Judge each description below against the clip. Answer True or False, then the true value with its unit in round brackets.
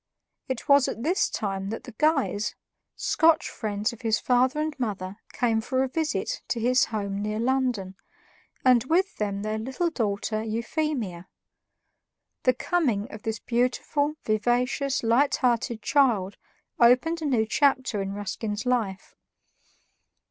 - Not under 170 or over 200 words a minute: False (140 wpm)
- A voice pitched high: True (235 Hz)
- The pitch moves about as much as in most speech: True (4.0 semitones)